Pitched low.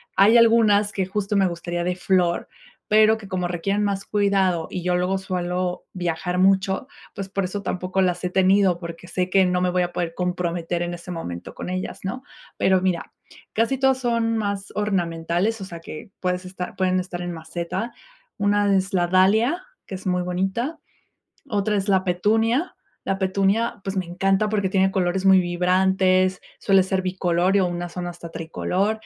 No: medium, 185 Hz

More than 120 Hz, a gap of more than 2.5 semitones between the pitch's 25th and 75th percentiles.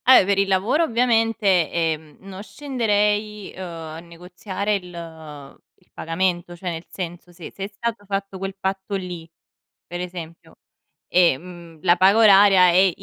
Yes: medium, 185 Hz; average, 2.9 semitones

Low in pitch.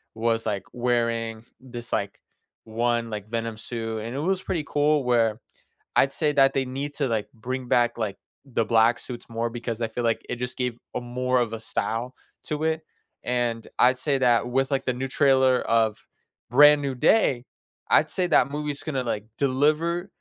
Yes: low, 125 Hz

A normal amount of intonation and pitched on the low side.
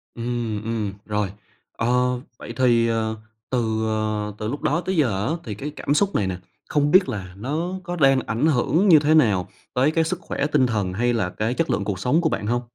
No: wide, 5.7 semitones; low, 120 Hz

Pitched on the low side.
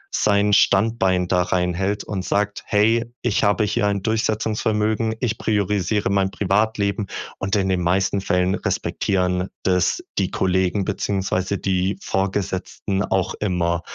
Yes: low, 100 Hz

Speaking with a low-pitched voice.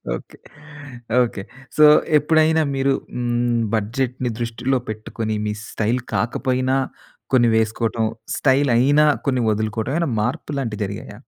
Yes: low, 120 Hz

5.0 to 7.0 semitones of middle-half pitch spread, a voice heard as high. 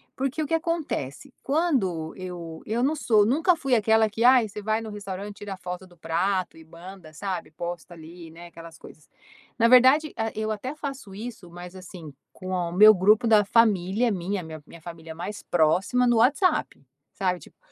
Yes: wide, 5.4 semitones; high, 200 Hz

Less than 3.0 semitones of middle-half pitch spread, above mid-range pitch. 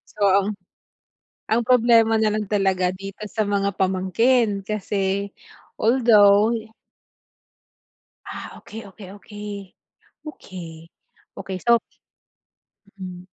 Yes: narrow, 2.5 semitones; high, 200 Hz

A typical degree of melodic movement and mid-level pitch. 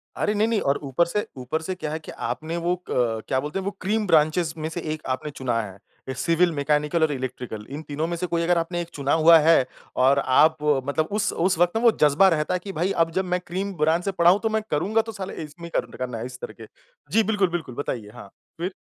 Yes: average, 4.2 semitones; medium, 165 Hz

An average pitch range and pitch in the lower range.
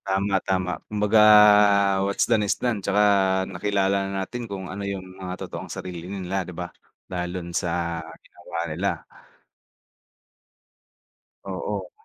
No: narrow, 1.7 semitones; very low, 95 Hz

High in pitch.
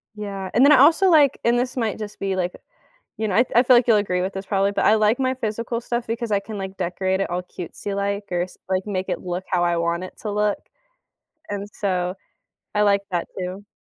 Yes: high, 200 Hz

